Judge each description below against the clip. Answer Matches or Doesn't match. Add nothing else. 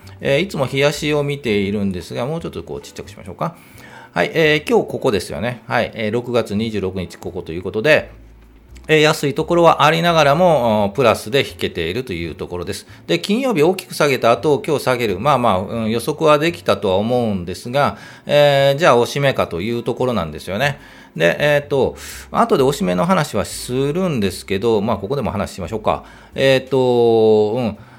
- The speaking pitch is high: Doesn't match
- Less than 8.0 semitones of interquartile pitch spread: Matches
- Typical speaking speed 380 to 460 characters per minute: Matches